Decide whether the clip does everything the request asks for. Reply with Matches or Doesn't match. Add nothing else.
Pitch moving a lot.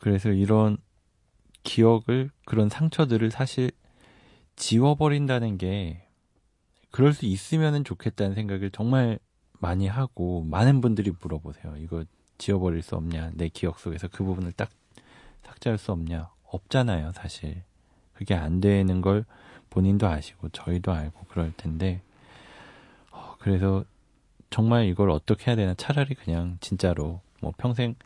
Doesn't match